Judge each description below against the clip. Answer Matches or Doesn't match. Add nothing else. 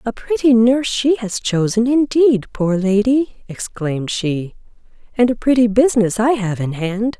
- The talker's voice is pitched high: Matches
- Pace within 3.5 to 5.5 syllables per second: Matches